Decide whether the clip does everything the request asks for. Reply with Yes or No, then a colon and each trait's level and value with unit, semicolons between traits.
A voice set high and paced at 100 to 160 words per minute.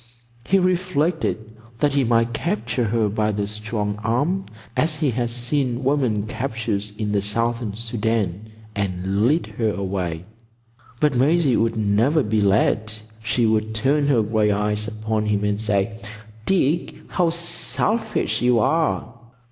No: low, 115 Hz; average, 140 wpm